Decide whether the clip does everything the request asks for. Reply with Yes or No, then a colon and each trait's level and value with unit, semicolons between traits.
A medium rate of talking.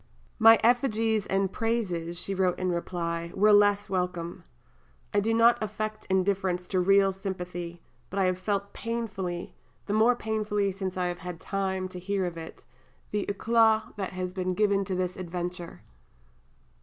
Yes: average, 160 wpm